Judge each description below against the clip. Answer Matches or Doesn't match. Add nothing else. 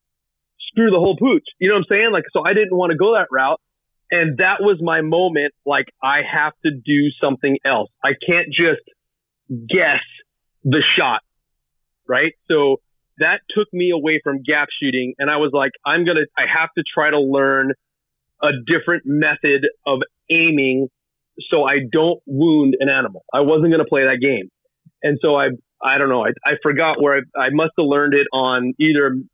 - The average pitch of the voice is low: Doesn't match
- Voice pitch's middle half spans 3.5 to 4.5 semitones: Matches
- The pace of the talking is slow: Doesn't match